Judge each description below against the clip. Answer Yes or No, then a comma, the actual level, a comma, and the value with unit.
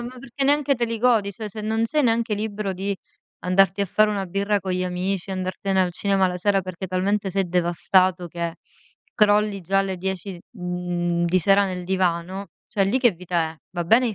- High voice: Yes, high, 195 Hz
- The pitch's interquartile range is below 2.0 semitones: No, average, 2.7 semitones